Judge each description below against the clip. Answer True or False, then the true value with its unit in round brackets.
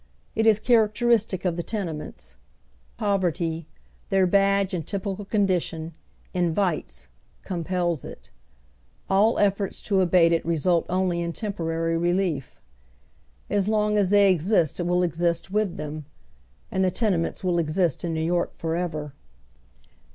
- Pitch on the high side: False (180 Hz)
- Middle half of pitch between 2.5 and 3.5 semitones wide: True (3.1 semitones)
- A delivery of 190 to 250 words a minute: False (145 wpm)